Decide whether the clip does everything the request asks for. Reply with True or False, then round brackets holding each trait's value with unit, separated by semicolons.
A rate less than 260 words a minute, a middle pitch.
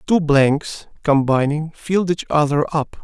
True (140 wpm; 150 Hz)